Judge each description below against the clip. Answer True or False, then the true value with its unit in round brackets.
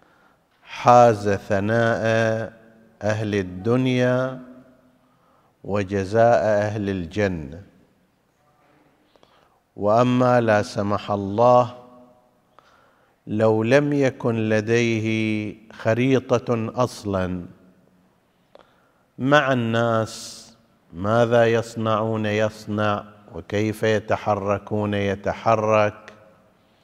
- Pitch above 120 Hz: False (110 Hz)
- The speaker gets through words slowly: True (55 wpm)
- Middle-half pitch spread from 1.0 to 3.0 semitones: True (2.6 semitones)